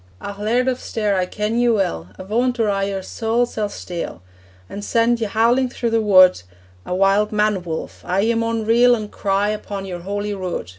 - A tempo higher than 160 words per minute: Yes, average, 200 wpm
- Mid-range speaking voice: No, high, 210 Hz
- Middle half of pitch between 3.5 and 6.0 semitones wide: No, average, 2.8 semitones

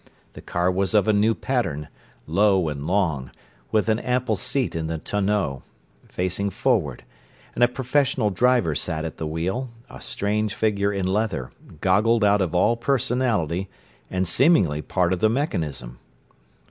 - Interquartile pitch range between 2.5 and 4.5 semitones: No, average, 5.1 semitones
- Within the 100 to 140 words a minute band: No, average, 155 wpm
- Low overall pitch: Yes, low, 100 Hz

